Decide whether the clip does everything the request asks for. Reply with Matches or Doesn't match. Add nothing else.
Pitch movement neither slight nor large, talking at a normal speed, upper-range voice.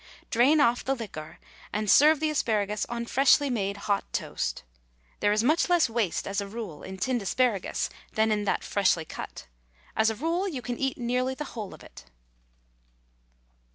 Matches